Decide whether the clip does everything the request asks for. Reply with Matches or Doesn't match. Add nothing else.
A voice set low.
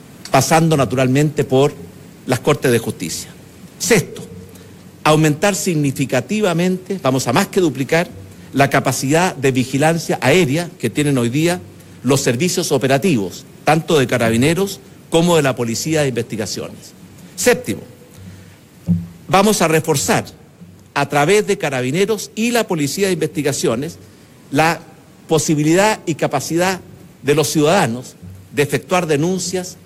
Doesn't match